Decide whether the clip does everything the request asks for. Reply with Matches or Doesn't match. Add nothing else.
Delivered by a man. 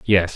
Matches